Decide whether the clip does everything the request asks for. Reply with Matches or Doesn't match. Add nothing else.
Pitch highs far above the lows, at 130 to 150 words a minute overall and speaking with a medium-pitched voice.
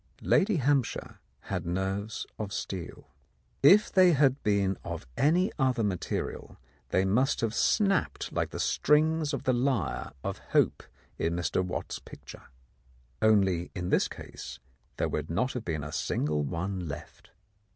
Doesn't match